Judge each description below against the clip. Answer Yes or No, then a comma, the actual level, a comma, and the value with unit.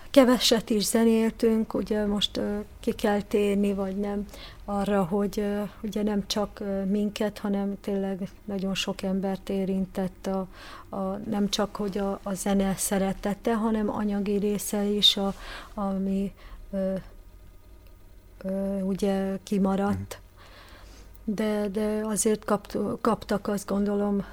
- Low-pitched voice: No, high, 200 Hz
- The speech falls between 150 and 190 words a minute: No, average, 125 wpm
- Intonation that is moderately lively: No, narrow, 1.5 semitones